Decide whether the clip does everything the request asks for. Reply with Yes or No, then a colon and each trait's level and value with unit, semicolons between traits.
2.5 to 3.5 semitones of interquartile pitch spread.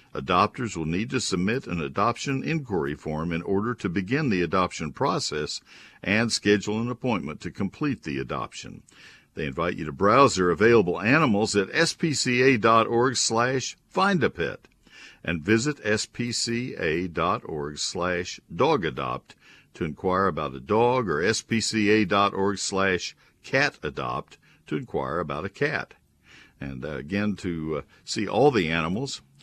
No: average, 5.3 semitones